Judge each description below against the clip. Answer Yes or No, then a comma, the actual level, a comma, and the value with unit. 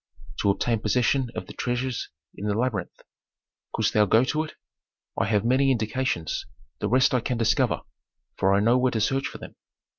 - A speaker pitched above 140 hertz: No, low, 120 Hz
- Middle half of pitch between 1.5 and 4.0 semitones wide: Yes, average, 3.4 semitones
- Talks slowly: No, average, 185 wpm